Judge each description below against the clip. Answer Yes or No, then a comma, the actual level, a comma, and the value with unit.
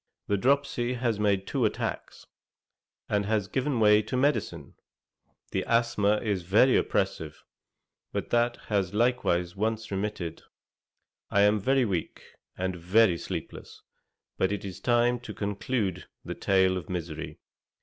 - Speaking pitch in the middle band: No, low, 105 Hz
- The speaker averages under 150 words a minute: Yes, slow, 135 wpm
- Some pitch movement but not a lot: Yes, average, 4.1 semitones